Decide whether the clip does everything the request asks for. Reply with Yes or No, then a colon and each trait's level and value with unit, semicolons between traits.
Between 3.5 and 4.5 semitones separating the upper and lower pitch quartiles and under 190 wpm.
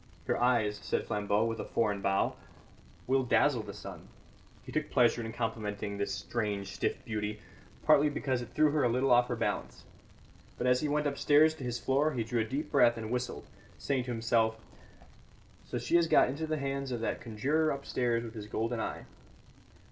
No: average, 3.8 semitones; average, 195 wpm